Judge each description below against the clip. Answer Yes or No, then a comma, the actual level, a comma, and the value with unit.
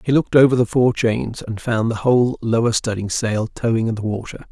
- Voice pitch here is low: Yes, low, 115 Hz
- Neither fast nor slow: No, fast, 225 wpm